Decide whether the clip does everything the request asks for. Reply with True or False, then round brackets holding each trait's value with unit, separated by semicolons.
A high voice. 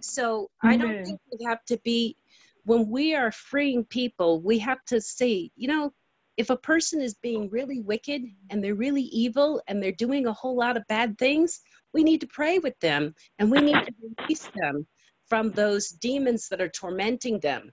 True (235 Hz)